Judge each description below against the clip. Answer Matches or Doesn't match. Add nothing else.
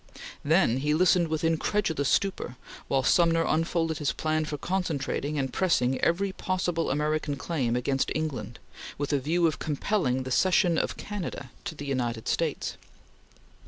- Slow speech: Doesn't match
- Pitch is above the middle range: Doesn't match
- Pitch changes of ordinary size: Matches